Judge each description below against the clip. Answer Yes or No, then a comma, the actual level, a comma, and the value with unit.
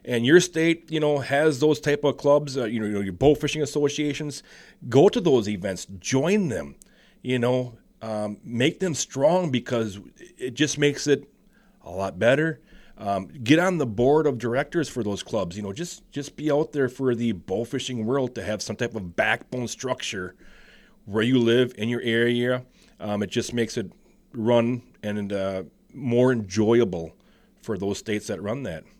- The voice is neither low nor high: No, low, 125 Hz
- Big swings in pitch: No, average, 4.8 semitones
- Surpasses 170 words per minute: Yes, average, 180 wpm